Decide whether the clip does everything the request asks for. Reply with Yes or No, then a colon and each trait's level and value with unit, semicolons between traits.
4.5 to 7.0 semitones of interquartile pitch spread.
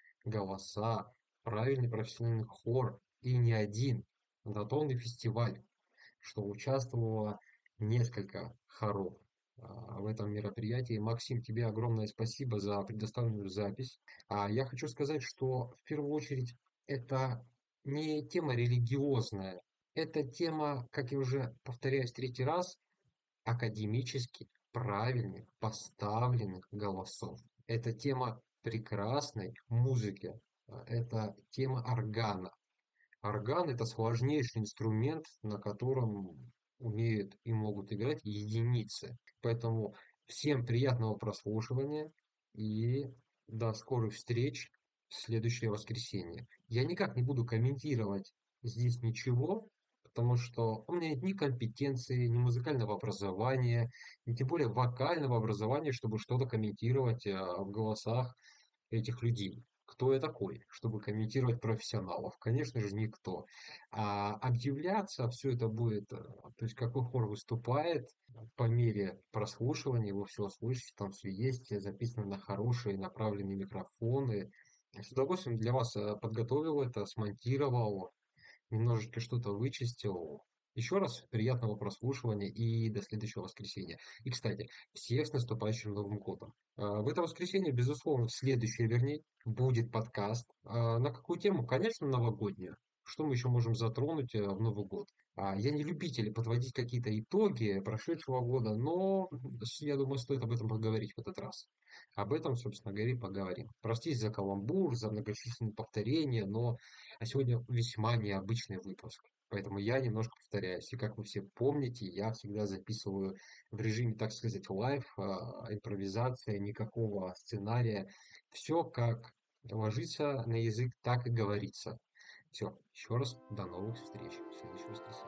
No: average, 3.3 semitones